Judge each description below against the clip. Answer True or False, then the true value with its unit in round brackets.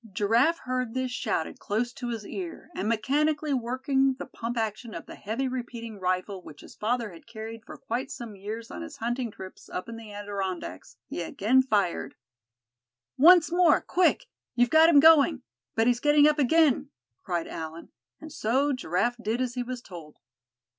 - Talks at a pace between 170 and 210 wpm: True (175 wpm)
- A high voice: True (240 Hz)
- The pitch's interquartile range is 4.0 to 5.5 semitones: True (4.3 semitones)